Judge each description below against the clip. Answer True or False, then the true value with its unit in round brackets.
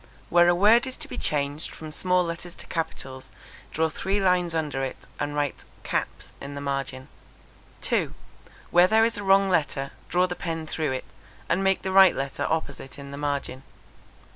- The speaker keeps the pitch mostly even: False (4.5 semitones)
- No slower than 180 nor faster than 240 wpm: True (185 wpm)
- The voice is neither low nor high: True (160 Hz)